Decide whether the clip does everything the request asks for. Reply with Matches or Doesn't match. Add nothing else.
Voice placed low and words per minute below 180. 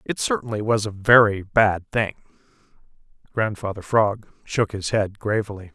Matches